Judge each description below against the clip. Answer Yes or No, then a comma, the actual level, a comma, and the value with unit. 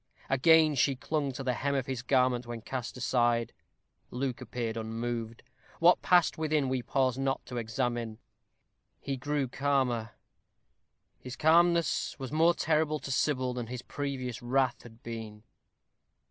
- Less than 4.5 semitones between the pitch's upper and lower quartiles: Yes, average, 3.0 semitones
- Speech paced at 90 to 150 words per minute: Yes, average, 145 wpm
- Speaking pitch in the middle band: No, low, 130 Hz